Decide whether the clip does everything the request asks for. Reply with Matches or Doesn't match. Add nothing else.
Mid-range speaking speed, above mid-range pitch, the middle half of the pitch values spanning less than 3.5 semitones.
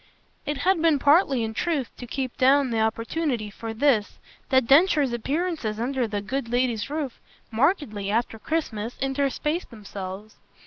Doesn't match